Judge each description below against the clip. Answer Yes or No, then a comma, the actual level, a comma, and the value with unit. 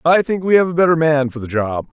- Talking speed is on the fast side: Yes, fast, 335 wpm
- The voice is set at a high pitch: No, medium, 155 Hz